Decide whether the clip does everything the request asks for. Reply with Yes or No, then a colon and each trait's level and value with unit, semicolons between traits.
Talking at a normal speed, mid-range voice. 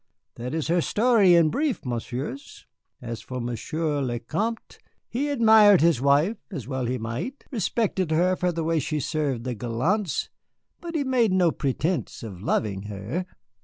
Yes: average, 165 wpm; medium, 160 Hz